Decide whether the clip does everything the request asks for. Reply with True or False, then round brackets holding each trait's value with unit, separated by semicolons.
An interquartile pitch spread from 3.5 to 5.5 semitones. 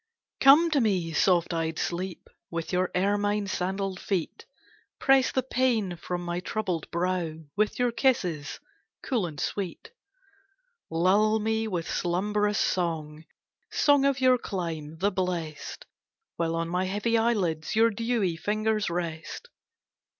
True (4.5 semitones)